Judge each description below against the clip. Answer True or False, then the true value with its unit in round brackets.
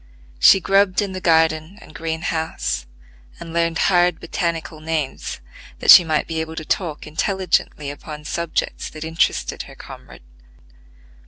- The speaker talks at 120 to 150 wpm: True (145 wpm)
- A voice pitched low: False (160 Hz)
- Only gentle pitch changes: True (2.0 semitones)